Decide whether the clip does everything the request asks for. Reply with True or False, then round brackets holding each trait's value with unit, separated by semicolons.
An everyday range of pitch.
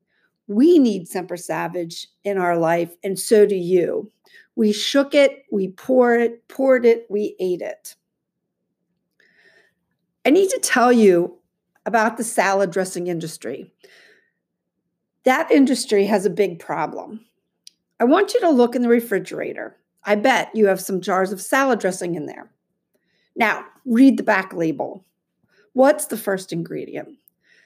False (6.0 semitones)